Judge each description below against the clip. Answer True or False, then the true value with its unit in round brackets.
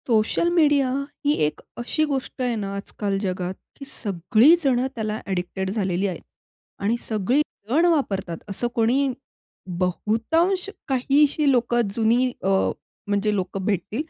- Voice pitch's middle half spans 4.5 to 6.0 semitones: True (5.5 semitones)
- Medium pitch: False (225 Hz)